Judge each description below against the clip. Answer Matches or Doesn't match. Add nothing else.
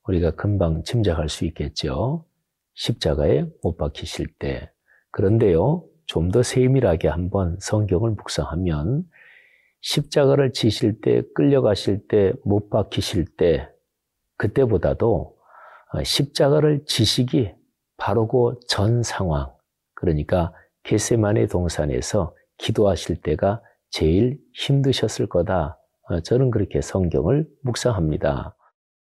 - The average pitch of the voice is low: Matches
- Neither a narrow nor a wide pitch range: Doesn't match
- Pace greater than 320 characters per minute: Doesn't match